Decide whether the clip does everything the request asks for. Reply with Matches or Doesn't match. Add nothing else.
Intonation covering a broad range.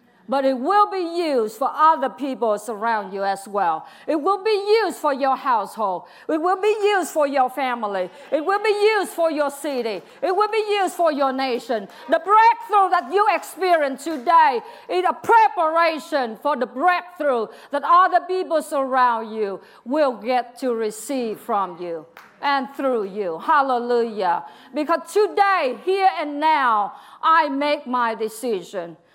Matches